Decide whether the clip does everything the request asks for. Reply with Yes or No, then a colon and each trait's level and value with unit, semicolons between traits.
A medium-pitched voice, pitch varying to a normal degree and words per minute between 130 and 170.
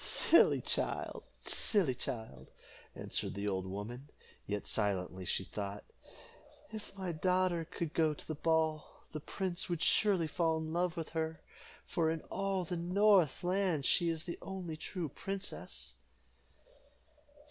Yes: medium, 165 Hz; average, 4.6 semitones; average, 140 wpm